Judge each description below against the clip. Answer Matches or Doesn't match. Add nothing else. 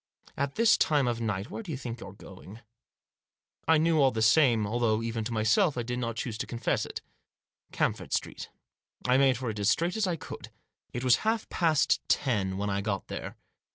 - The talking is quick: Matches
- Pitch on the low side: Matches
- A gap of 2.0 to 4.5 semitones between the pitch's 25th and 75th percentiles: Doesn't match